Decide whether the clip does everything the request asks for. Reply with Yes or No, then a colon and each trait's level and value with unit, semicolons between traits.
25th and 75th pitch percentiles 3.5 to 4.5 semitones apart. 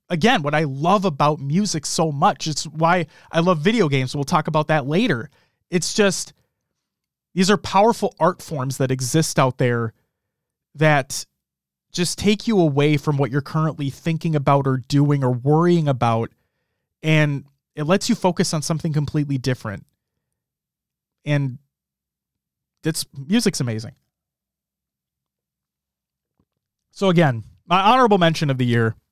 No: average, 4.9 semitones